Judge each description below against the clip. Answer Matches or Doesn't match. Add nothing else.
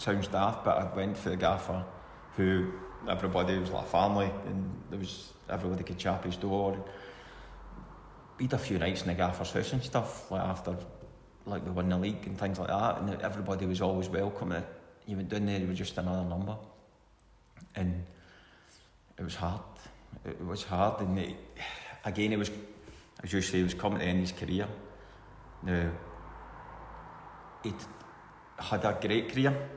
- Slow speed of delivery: Doesn't match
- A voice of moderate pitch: Doesn't match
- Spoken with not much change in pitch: Matches